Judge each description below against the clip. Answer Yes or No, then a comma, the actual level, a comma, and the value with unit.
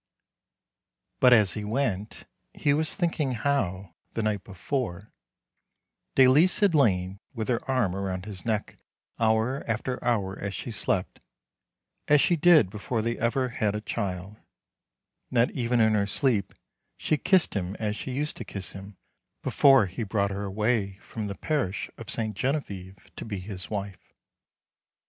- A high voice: No, low, 110 Hz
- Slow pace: No, average, 155 wpm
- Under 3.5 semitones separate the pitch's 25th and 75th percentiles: No, average, 4.5 semitones